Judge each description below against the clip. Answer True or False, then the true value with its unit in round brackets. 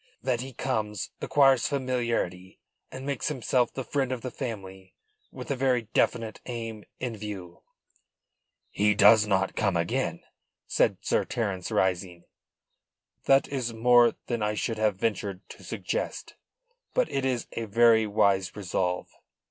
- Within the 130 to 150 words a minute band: True (140 wpm)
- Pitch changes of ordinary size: True (4.2 semitones)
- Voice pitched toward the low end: True (115 Hz)